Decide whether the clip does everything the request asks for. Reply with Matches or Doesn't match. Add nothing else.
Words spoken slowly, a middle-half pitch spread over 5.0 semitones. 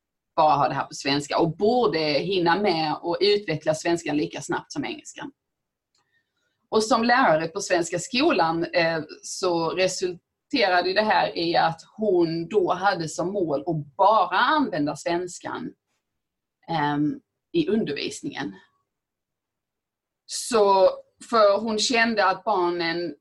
Doesn't match